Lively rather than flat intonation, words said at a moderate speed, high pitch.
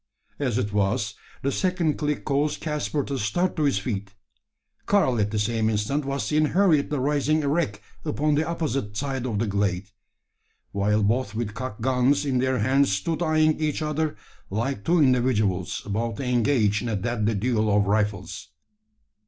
No: wide, 5.9 semitones; average, 170 wpm; low, 125 Hz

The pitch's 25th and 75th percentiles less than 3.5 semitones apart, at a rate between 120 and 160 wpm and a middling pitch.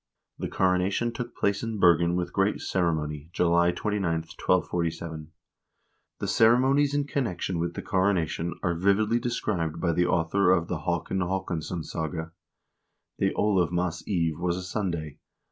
No: average, 3.0 semitones; average, 140 wpm; very low, 90 Hz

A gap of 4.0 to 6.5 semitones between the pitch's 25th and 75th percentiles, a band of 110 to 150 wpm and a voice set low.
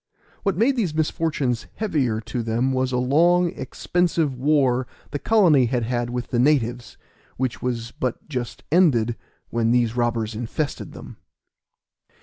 Yes: average, 4.6 semitones; average, 140 wpm; low, 130 Hz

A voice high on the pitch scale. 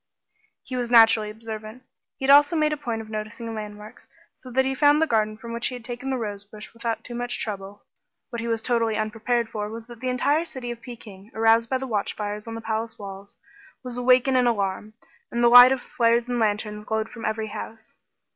Yes: high, 230 Hz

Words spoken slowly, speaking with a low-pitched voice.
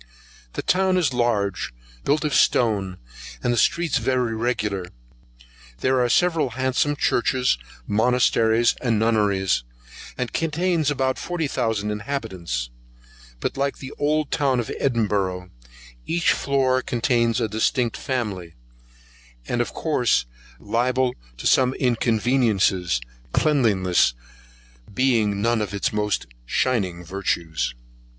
Yes: slow, 115 wpm; low, 120 Hz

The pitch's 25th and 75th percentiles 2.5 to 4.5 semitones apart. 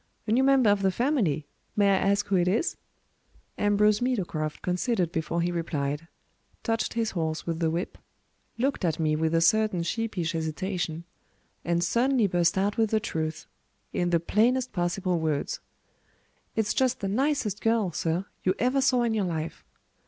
No: average, 5.2 semitones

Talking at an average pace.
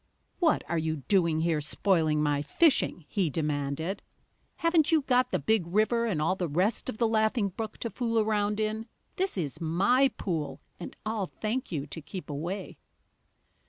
Yes: average, 170 wpm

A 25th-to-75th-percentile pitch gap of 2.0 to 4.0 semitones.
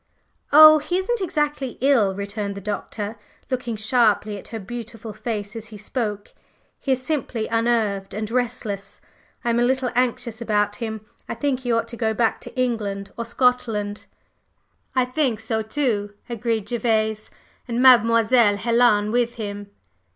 Yes: average, 2.9 semitones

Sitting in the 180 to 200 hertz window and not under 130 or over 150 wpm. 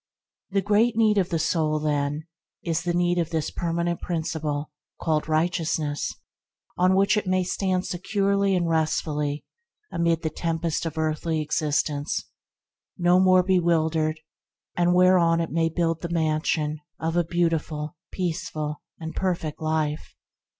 No: medium, 165 Hz; slow, 135 wpm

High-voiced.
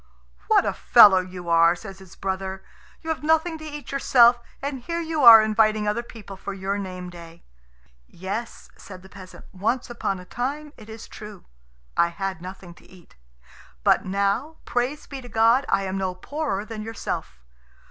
Yes: high, 210 Hz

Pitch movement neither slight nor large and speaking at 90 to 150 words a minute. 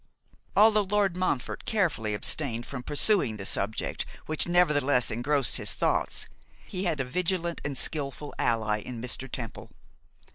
No: wide, 6.9 semitones; average, 140 wpm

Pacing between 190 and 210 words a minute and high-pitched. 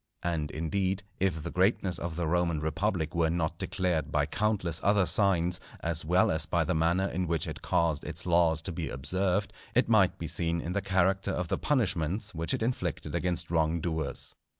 No: average, 195 wpm; very low, 85 Hz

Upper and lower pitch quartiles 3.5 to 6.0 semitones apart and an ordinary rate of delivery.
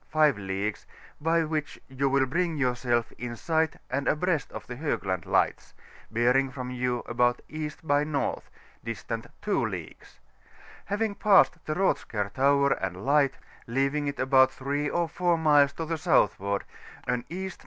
Yes: average, 4.4 semitones; average, 155 wpm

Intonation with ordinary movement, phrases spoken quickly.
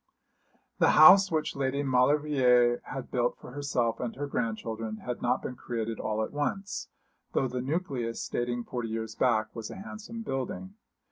No: average, 3.8 semitones; average, 160 wpm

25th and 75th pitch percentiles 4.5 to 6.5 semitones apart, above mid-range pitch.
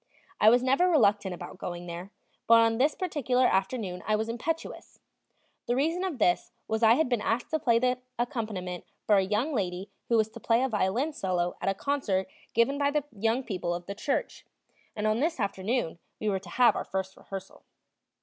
Yes: average, 5.1 semitones; high, 225 Hz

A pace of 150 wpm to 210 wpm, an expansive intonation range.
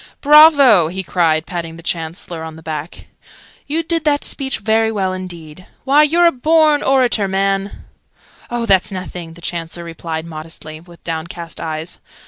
Yes: average, 155 wpm; wide, 7.5 semitones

